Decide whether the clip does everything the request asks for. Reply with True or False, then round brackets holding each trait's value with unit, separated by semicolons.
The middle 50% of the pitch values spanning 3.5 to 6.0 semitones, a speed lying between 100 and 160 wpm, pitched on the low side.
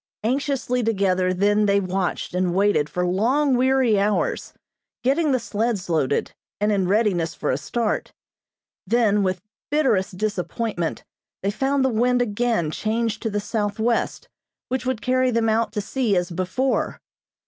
False (4.5 semitones; 150 wpm; 215 Hz)